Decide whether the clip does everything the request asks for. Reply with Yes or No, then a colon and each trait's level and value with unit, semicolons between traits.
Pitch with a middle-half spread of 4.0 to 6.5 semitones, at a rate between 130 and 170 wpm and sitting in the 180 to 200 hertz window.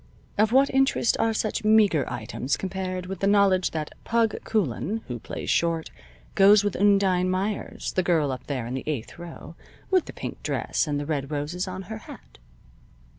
No: wide, 5.5 semitones; average, 180 wpm; medium, 185 Hz